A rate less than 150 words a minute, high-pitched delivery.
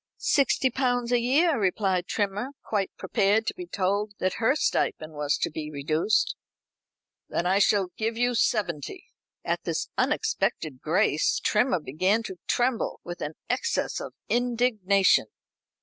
Yes: average, 140 wpm; high, 205 Hz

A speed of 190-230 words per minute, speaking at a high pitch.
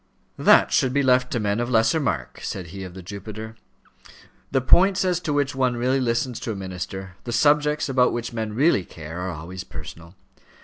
No: average, 195 wpm; low, 115 Hz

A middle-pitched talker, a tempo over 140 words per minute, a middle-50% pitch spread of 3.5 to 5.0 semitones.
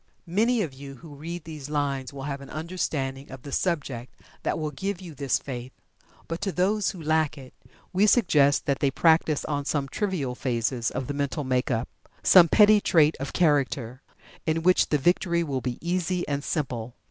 Yes: medium, 145 Hz; average, 190 wpm; average, 4.2 semitones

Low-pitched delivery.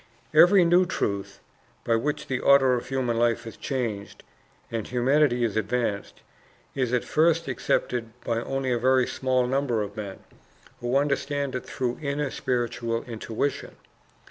Yes: low, 125 Hz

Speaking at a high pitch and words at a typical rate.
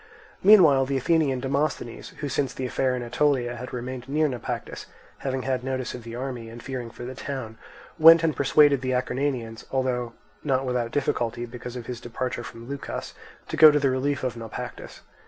No: low, 130 Hz; average, 185 wpm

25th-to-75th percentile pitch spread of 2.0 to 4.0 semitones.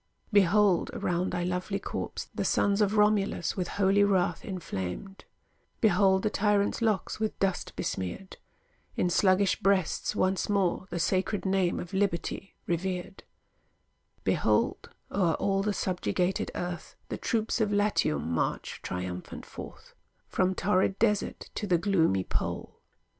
Yes: narrow, 2.4 semitones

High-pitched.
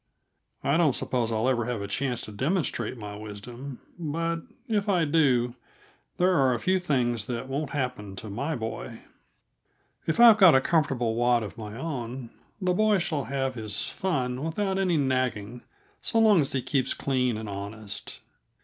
No: low, 130 Hz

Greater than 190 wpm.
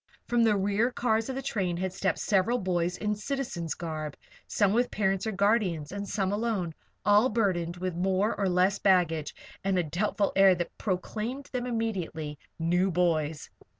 No: average, 175 wpm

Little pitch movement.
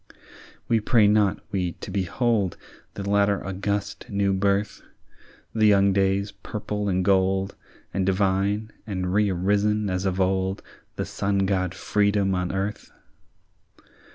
Yes: narrow, 1.3 semitones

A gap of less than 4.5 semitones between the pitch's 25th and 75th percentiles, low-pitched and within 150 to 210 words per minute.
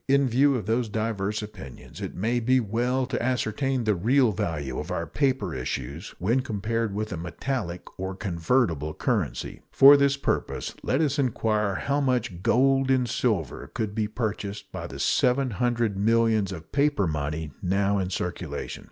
No: average, 5.2 semitones; low, 110 Hz; average, 165 wpm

